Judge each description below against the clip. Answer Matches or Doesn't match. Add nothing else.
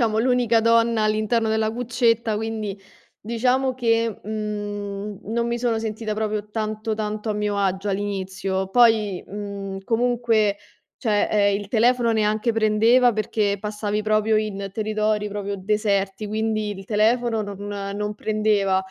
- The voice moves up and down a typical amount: Doesn't match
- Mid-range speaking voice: Doesn't match